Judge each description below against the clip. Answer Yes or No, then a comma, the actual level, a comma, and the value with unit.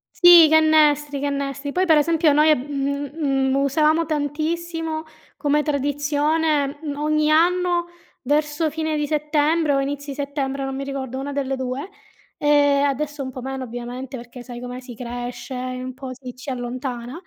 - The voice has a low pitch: No, very high, 285 Hz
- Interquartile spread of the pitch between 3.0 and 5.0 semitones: No, narrow, 2.6 semitones